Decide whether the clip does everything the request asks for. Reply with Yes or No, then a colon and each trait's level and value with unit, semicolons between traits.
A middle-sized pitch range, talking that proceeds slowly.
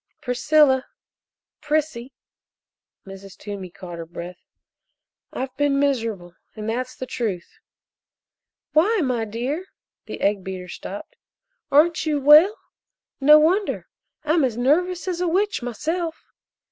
No: wide, 6.8 semitones; slow, 120 wpm